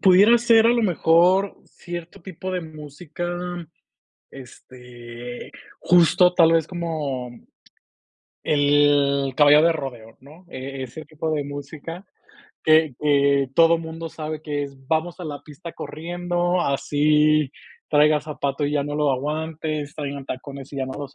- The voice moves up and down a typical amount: Yes, average, 3.1 semitones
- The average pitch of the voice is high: No, medium, 150 Hz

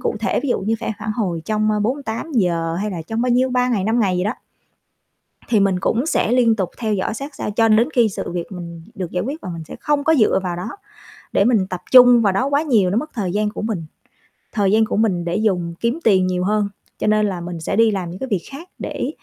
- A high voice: Yes, high, 215 Hz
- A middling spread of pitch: Yes, average, 4.5 semitones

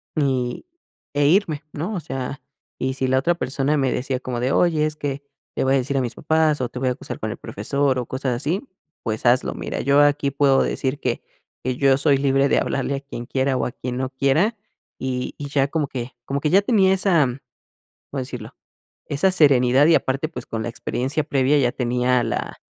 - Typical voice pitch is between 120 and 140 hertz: Yes, low, 135 Hz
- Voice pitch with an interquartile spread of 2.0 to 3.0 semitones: Yes, narrow, 2.5 semitones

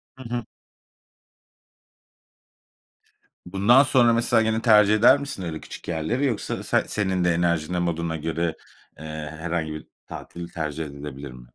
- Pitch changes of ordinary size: No, wide, 5.9 semitones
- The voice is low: Yes, very low, 85 Hz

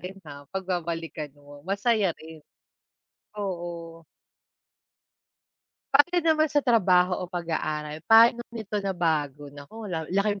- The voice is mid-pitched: Yes, medium, 175 Hz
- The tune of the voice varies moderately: Yes, average, 4.8 semitones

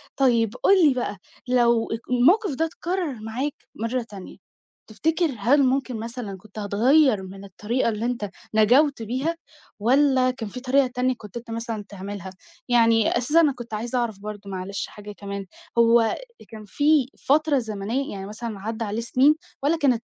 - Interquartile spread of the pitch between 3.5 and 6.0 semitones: Yes, average, 4.1 semitones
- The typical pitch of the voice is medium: No, high, 235 Hz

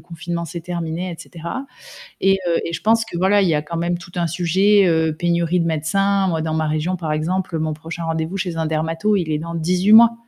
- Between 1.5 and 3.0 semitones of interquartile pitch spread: Yes, narrow, 2.4 semitones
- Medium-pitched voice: Yes, medium, 170 Hz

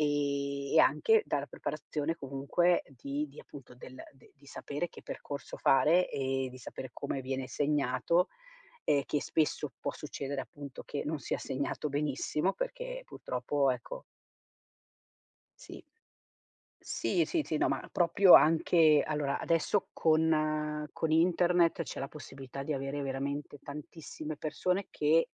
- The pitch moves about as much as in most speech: Yes, average, 3.0 semitones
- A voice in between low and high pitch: Yes, medium, 150 Hz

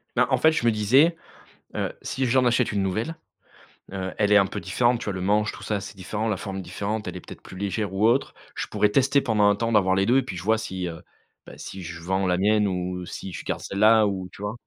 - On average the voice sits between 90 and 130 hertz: Yes, low, 105 Hz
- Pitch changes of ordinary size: Yes, average, 3.4 semitones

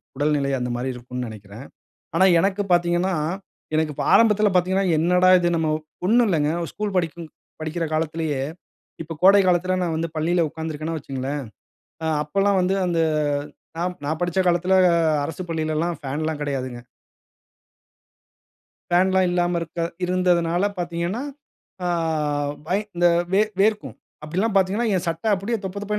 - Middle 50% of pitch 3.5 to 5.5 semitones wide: No, average, 3.1 semitones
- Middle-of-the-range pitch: Yes, medium, 170 Hz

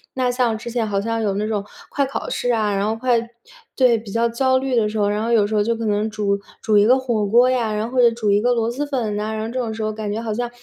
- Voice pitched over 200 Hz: Yes, high, 225 Hz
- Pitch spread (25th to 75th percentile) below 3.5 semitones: Yes, narrow, 2.4 semitones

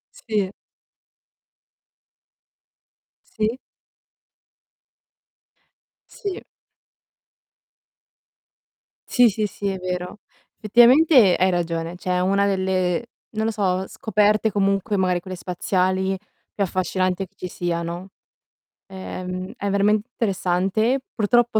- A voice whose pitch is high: Yes, high, 195 Hz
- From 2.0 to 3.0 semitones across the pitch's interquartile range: Yes, average, 2.7 semitones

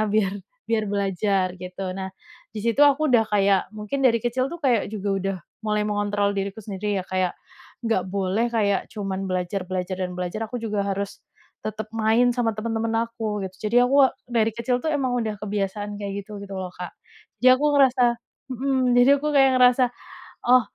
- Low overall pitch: No, high, 210 Hz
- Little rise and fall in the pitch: No, average, 3.4 semitones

